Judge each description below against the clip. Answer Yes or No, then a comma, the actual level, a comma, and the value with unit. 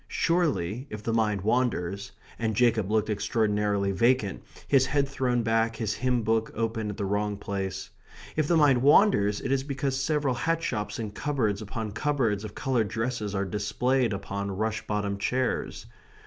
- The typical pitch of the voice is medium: No, low, 110 Hz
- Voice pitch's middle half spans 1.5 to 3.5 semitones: No, average, 4.0 semitones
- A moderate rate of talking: Yes, average, 165 wpm